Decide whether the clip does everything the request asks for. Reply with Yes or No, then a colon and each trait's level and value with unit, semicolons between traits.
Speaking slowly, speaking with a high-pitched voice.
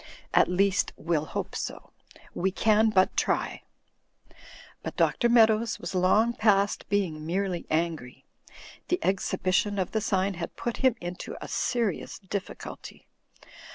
Yes: slow, 130 wpm; high, 195 Hz